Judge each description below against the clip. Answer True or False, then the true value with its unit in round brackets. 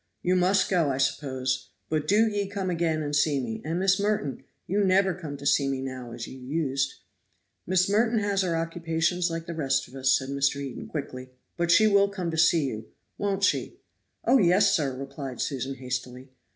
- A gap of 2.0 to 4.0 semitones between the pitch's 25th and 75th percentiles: False (5.6 semitones)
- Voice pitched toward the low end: False (160 Hz)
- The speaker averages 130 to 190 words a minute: False (200 wpm)